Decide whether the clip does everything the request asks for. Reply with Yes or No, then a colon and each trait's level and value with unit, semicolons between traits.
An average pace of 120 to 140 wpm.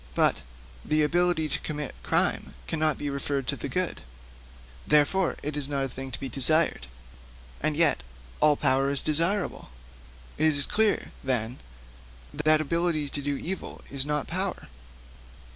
No: average, 150 wpm